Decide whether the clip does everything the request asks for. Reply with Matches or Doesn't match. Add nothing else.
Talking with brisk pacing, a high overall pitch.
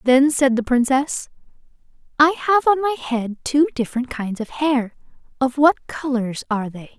Doesn't match